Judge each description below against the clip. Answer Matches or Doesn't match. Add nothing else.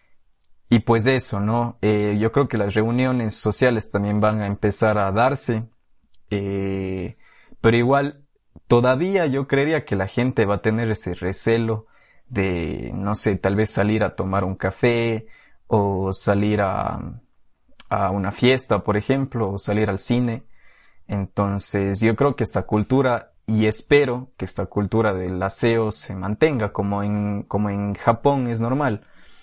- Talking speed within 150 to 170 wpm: Matches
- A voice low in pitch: Matches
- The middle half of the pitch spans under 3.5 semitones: Matches